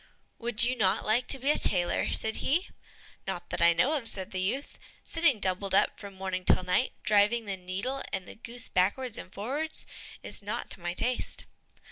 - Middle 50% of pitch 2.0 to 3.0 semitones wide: No, average, 5.0 semitones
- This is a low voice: No, high, 210 Hz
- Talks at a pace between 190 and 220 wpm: Yes, average, 195 wpm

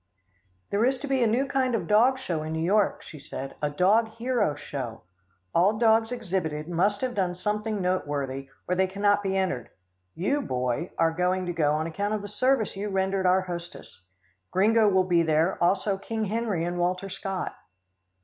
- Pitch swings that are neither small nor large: Yes, average, 4.2 semitones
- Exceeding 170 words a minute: Yes, average, 190 wpm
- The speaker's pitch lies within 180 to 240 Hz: Yes, high, 190 Hz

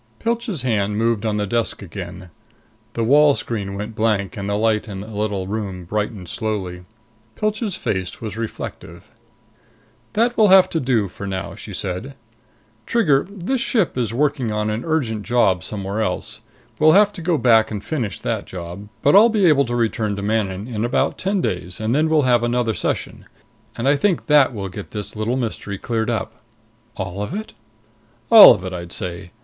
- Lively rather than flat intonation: Yes, wide, 6.0 semitones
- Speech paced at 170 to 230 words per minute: Yes, average, 185 wpm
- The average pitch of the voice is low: Yes, low, 110 Hz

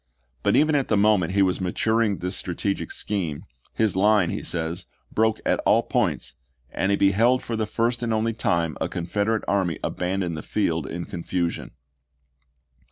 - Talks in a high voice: No, low, 100 Hz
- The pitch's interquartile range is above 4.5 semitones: No, average, 4.2 semitones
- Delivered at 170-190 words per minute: Yes, average, 175 wpm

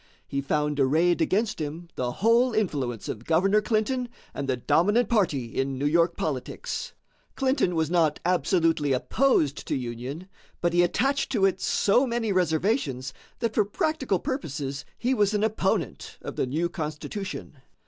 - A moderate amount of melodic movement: No, wide, 6.8 semitones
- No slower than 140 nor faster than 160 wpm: Yes, average, 155 wpm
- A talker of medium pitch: Yes, medium, 175 Hz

